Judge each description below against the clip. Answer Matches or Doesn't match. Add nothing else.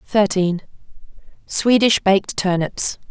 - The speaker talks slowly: Matches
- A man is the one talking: Doesn't match